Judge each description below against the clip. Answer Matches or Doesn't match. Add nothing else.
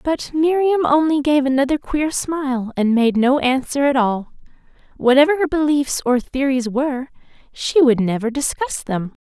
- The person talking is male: Doesn't match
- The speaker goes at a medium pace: Matches